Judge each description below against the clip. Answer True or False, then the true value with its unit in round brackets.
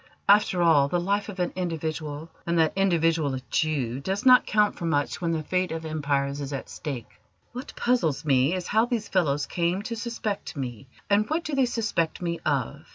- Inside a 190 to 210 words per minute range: True (200 wpm)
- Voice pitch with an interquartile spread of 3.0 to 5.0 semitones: False (5.6 semitones)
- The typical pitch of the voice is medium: True (170 Hz)